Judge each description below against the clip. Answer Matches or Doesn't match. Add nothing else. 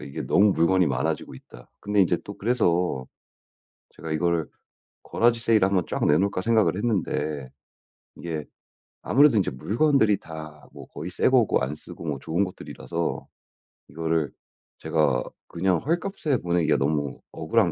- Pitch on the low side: Matches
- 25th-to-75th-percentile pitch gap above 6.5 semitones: Doesn't match